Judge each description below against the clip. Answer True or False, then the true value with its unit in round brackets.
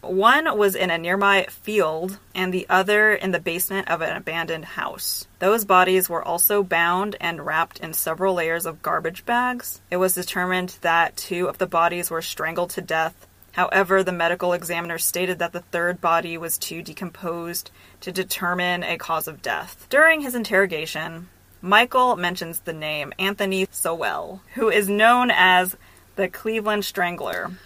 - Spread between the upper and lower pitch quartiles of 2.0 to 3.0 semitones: True (2.6 semitones)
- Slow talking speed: False (165 wpm)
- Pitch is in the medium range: True (180 Hz)